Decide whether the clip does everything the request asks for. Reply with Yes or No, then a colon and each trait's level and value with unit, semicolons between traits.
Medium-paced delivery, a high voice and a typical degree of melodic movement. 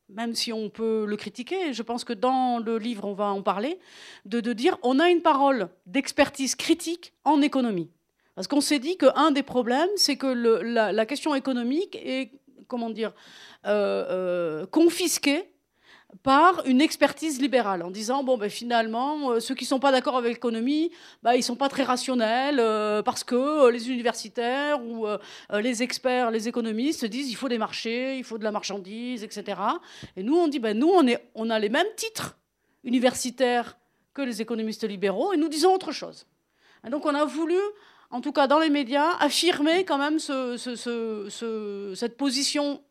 Yes: average, 195 wpm; very high, 255 Hz; average, 4.3 semitones